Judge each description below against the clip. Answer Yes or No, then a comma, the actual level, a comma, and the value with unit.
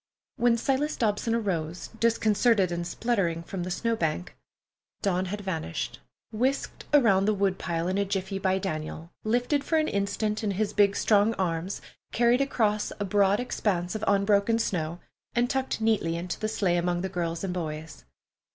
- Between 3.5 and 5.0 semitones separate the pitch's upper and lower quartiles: Yes, average, 4.1 semitones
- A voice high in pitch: Yes, high, 200 Hz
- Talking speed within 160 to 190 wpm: Yes, average, 165 wpm